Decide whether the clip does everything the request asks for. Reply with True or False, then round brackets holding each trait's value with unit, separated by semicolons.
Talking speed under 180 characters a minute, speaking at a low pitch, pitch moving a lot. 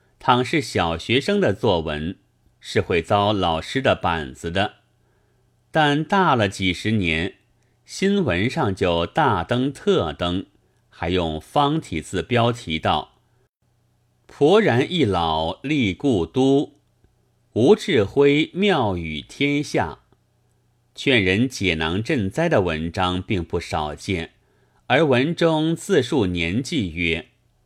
True (160 characters per minute; 120 Hz; 6.3 semitones)